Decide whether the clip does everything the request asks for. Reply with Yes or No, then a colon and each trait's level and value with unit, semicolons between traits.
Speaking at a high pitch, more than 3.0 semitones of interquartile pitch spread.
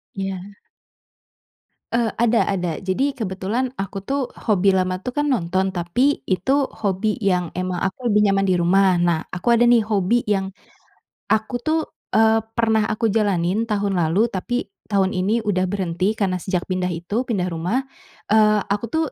Yes: high, 200 Hz; average, 3.6 semitones